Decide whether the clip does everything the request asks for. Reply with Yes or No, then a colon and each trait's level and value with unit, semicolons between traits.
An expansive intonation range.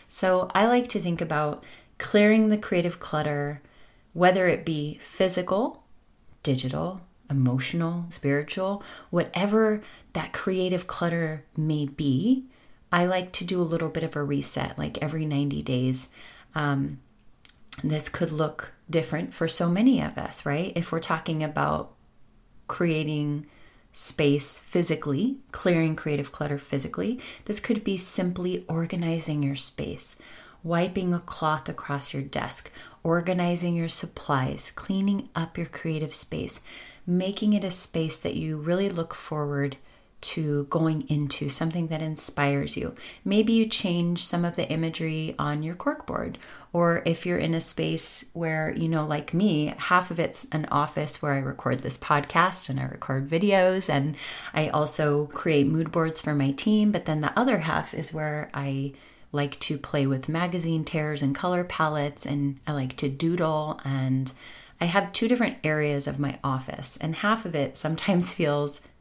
No: average, 3.6 semitones